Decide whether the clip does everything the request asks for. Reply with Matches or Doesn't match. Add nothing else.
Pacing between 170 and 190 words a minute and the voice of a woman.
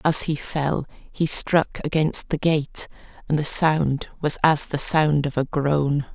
Matches